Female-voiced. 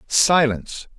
No: male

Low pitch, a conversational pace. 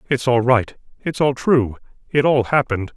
Yes: low, 125 Hz; average, 180 wpm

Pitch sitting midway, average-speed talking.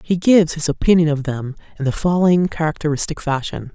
Yes: medium, 160 Hz; average, 175 wpm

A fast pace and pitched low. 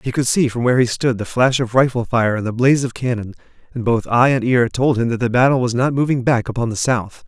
Yes: fast, 280 wpm; low, 120 Hz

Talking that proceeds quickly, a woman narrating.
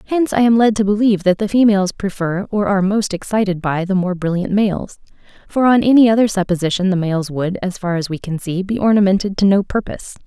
Yes: fast, 220 wpm; female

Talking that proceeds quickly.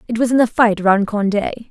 Yes: fast, 245 wpm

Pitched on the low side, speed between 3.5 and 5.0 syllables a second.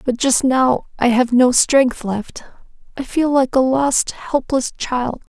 No: very high, 255 Hz; 3.6 syllables/s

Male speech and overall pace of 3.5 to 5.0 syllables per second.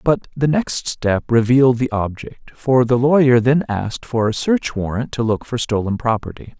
Yes: male; 4.7 syllables/s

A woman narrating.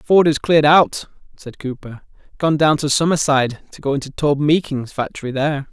No: male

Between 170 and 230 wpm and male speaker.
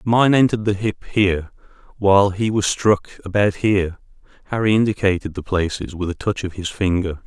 Yes: average, 175 wpm; male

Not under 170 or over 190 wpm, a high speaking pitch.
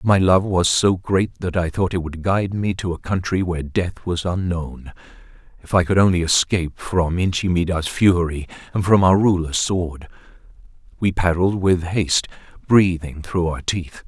No: average, 175 wpm; very low, 90 Hz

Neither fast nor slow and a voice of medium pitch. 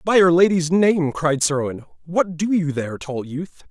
Yes: average, 195 wpm; medium, 165 Hz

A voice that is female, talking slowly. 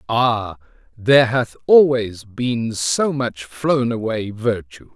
No: male; slow, 120 wpm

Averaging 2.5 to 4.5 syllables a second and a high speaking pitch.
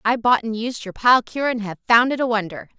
No: 5.5 syllables/s; high, 230 Hz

